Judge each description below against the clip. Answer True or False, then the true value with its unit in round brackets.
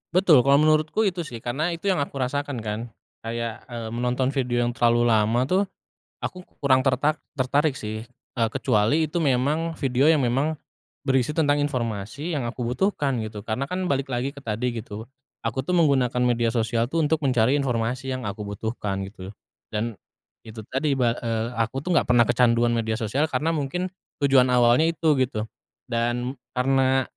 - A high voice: False (125 Hz)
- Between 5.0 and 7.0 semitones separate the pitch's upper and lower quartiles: False (3.7 semitones)